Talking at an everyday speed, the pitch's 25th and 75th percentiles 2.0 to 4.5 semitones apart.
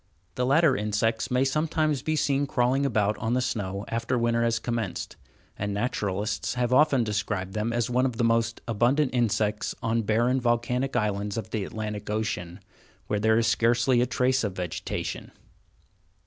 Yes: average, 165 wpm; average, 3.0 semitones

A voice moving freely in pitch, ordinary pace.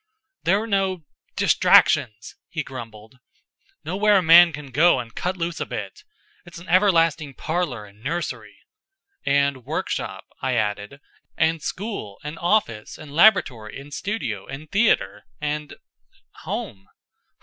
No: wide, 6.8 semitones; slow, 130 wpm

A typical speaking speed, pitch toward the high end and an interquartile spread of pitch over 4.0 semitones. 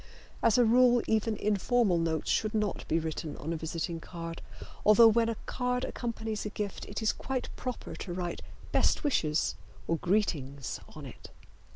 Yes: average, 170 wpm; high, 210 Hz; wide, 5.6 semitones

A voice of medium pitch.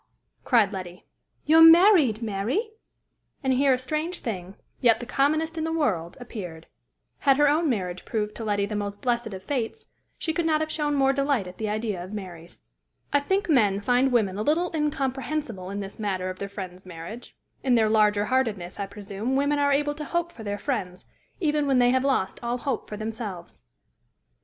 No: high, 235 Hz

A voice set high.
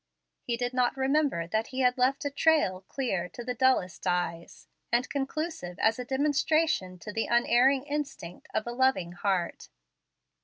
Yes: very high, 250 Hz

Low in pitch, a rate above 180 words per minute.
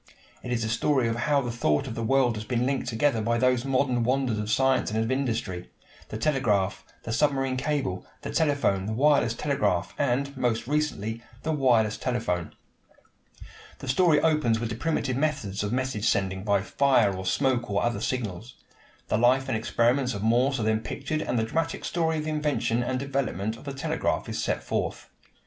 Yes: low, 125 Hz; average, 190 wpm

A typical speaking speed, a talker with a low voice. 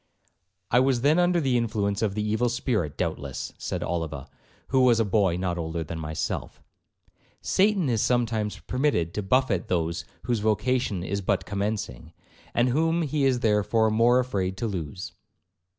Yes: average, 160 wpm; low, 110 Hz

